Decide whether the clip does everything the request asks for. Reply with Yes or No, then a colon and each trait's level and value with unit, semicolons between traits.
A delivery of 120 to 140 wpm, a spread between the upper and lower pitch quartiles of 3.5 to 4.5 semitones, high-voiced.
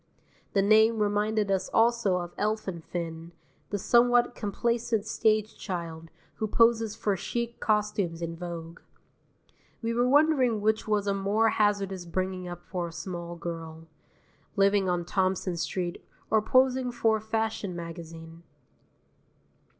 Yes: slow, 135 wpm; average, 4.1 semitones; high, 200 Hz